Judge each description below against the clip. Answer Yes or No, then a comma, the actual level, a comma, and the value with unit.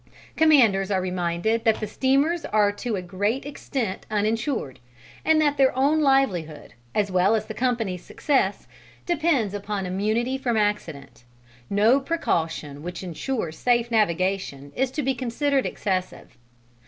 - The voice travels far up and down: Yes, wide, 6.2 semitones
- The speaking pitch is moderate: No, high, 215 Hz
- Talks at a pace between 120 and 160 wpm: Yes, average, 140 wpm